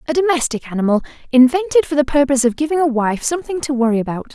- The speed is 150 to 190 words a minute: No, fast, 205 wpm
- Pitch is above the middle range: Yes, very high, 275 Hz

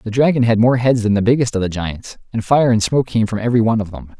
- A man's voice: Yes, male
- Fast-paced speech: Yes, fast, 300 wpm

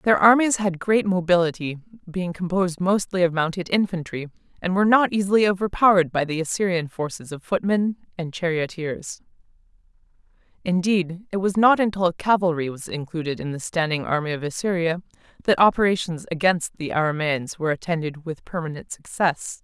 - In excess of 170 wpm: No, average, 145 wpm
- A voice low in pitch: No, medium, 175 Hz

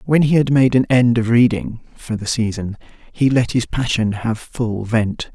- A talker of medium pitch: No, low, 120 Hz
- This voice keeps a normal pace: Yes, average, 180 wpm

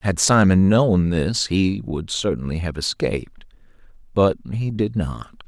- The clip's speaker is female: No, male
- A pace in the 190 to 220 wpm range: No, average, 140 wpm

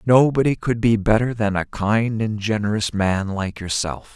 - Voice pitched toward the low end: Yes, low, 110 Hz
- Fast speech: No, average, 175 wpm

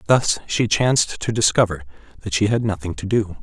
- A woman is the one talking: No, male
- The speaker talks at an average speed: Yes, average, 195 wpm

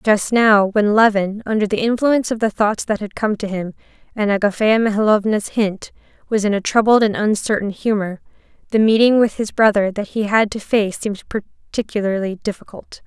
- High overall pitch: Yes, high, 210 Hz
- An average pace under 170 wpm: No, average, 180 wpm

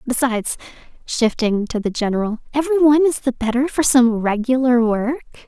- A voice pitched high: Yes, very high, 250 Hz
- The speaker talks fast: No, average, 140 wpm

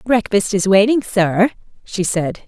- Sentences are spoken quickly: No, average, 145 wpm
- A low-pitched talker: No, high, 205 Hz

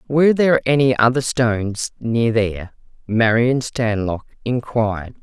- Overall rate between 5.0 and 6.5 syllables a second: No, 4.5 syllables/s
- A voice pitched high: No, low, 120 Hz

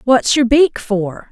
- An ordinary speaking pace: Yes, average, 185 wpm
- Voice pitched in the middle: No, high, 245 Hz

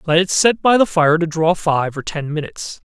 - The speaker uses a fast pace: Yes, fast, 245 wpm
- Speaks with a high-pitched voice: No, medium, 165 Hz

